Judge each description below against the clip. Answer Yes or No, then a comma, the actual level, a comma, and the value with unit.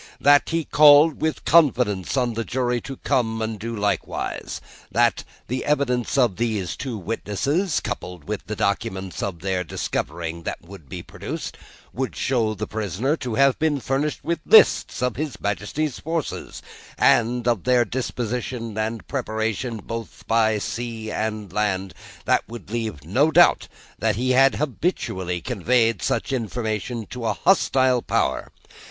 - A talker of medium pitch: No, low, 115 Hz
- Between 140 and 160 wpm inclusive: Yes, average, 150 wpm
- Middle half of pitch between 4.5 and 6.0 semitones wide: No, average, 3.9 semitones